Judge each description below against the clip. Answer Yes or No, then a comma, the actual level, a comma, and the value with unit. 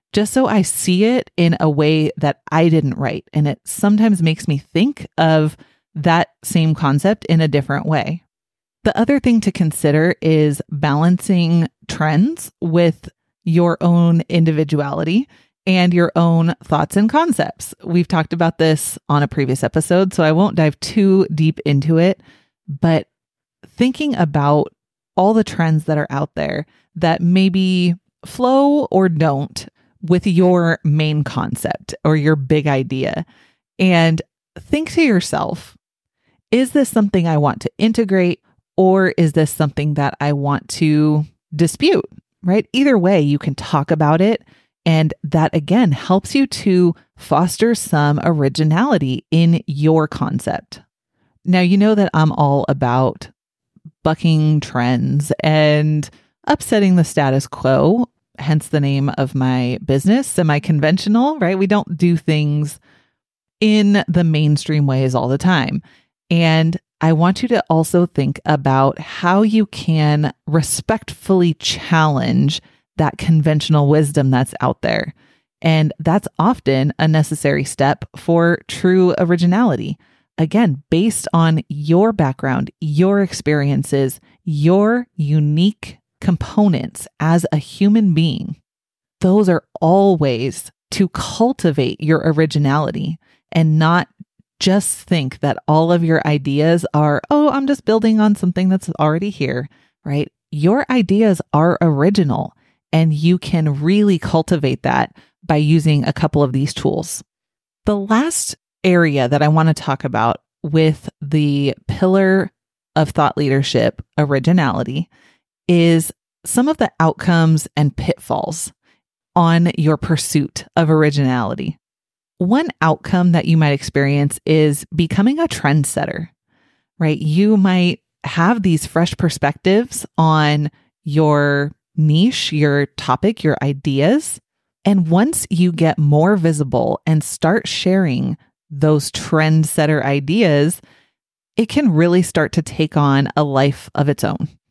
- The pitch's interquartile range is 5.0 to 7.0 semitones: No, average, 3.9 semitones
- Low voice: No, medium, 160 Hz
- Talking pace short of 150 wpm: Yes, slow, 135 wpm